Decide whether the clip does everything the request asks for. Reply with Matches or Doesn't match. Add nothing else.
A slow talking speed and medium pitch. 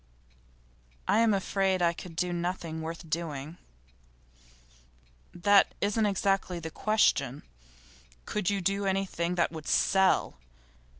Matches